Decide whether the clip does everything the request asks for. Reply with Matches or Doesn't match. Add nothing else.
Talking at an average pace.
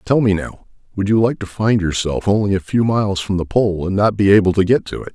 Doesn't match